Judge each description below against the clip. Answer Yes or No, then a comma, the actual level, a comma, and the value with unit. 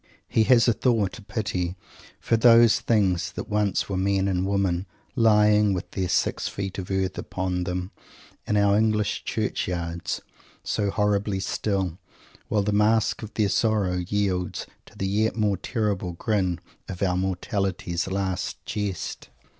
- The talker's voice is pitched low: Yes, low, 100 Hz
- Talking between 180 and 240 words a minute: No, average, 150 wpm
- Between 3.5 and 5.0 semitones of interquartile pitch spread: No, narrow, 2.4 semitones